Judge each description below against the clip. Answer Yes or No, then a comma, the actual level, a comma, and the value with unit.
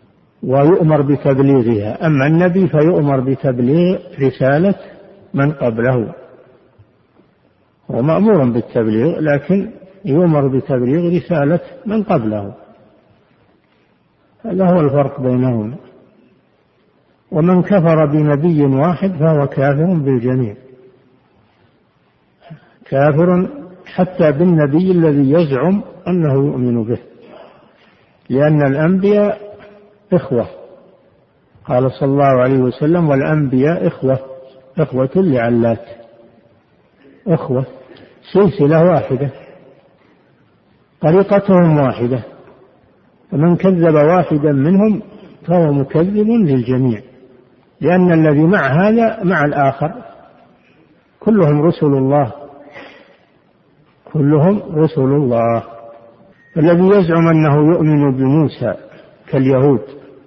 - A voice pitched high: No, medium, 150 Hz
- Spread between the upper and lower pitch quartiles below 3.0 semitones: No, average, 5.2 semitones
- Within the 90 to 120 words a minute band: No, average, 80 wpm